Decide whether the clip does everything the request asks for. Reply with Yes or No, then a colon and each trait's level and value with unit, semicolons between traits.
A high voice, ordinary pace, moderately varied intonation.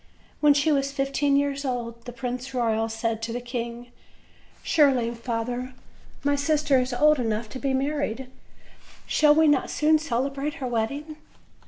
Yes: very high, 260 Hz; average, 155 wpm; average, 3.3 semitones